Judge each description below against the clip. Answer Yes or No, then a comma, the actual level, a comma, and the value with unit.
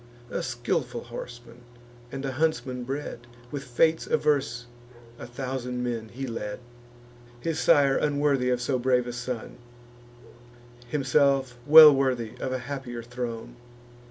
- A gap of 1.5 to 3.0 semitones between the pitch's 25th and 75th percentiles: Yes, narrow, 2.4 semitones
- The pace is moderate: No, slow, 130 wpm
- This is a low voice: Yes, low, 125 Hz